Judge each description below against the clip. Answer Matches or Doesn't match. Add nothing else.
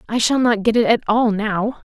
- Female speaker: Matches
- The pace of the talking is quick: Matches